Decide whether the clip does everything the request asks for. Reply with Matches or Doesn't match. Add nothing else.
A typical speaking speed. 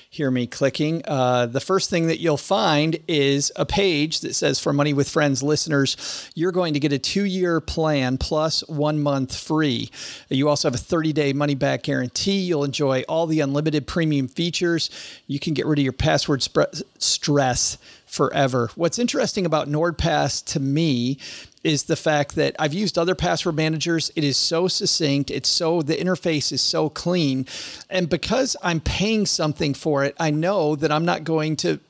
Matches